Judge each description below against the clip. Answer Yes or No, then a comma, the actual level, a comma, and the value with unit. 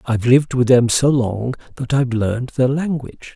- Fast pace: No, average, 195 wpm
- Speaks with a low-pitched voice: Yes, low, 125 Hz